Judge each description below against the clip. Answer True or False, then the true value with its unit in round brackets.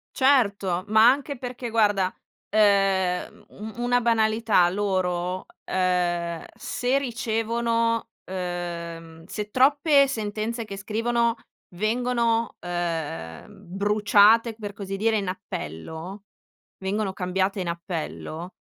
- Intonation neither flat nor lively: True (4.1 semitones)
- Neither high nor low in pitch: False (205 Hz)